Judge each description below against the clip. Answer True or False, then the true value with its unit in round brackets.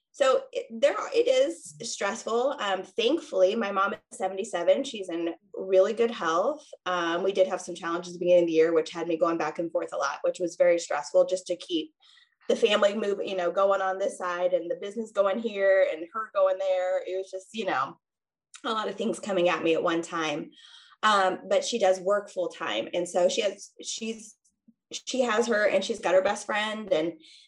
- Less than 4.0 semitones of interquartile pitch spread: False (4.8 semitones)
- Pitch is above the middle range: True (195 Hz)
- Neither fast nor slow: False (220 wpm)